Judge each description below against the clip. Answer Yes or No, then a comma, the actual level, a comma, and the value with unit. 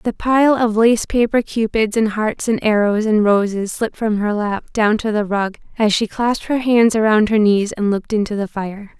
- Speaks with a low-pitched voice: No, high, 215 Hz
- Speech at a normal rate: No, fast, 220 wpm